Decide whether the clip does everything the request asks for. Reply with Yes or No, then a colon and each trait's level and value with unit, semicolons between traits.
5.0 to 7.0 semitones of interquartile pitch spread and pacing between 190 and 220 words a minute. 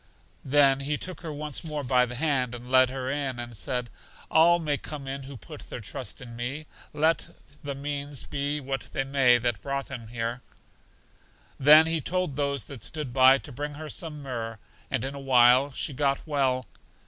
No: average, 2.7 semitones; average, 195 wpm